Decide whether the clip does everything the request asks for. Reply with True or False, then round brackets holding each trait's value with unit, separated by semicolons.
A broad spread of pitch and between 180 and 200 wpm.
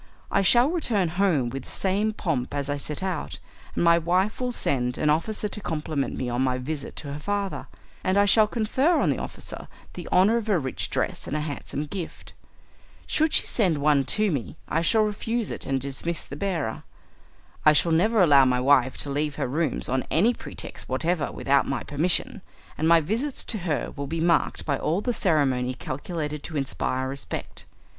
True (6.2 semitones; 195 wpm)